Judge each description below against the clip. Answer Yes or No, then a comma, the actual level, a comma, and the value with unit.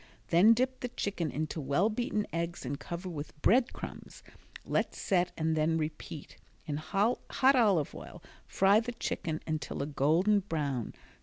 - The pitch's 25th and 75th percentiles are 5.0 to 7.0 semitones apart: Yes, wide, 5.4 semitones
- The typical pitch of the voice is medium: Yes, medium, 170 Hz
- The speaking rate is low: No, average, 155 wpm